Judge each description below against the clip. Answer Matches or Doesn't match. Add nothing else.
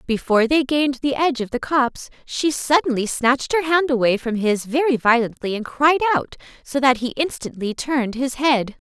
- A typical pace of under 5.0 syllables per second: Doesn't match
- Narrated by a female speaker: Matches